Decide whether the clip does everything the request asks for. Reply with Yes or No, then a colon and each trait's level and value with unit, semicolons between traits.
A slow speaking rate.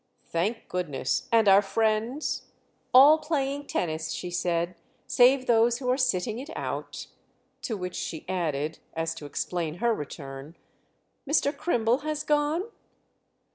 Yes: slow, 130 wpm